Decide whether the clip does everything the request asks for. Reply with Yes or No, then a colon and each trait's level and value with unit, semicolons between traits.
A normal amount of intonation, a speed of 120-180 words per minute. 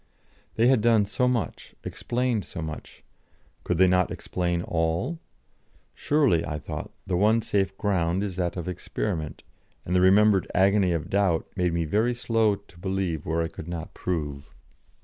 Yes: average, 3.9 semitones; average, 165 wpm